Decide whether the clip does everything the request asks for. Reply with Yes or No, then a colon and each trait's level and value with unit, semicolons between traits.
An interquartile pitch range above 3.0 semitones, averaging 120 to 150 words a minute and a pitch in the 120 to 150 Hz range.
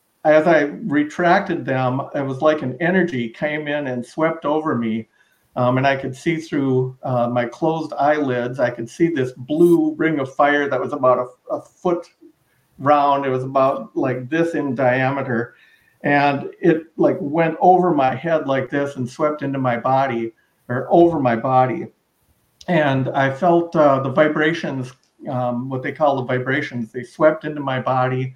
No: average, 3.4 semitones; average, 175 wpm; medium, 140 Hz